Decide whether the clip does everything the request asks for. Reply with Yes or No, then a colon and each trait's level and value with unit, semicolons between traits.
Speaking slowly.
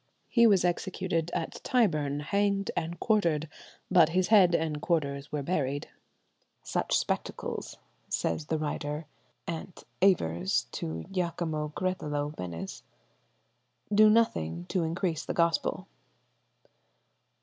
Yes: slow, 105 wpm